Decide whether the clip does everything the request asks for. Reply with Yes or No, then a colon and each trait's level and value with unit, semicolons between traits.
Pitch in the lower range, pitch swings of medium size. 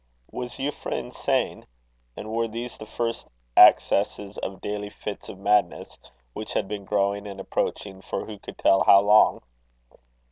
No: low, 105 Hz; narrow, 1.6 semitones